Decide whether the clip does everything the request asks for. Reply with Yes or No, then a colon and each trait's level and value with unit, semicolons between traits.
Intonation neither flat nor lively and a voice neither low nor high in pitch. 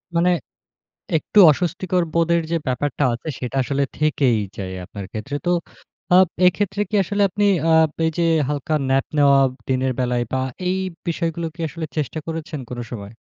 Yes: average, 4.7 semitones; medium, 155 Hz